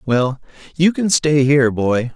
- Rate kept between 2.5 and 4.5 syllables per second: Yes, 4.1 syllables/s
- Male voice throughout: Yes, male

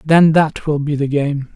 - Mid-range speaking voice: Yes, medium, 150 Hz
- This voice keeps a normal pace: No, fast, 230 wpm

